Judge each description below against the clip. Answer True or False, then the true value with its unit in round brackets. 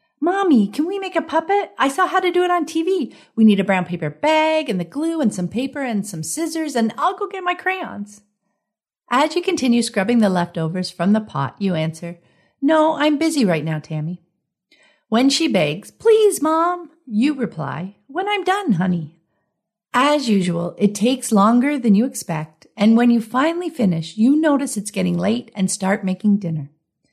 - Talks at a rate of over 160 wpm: True (190 wpm)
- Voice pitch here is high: True (225 Hz)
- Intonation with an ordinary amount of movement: False (8.9 semitones)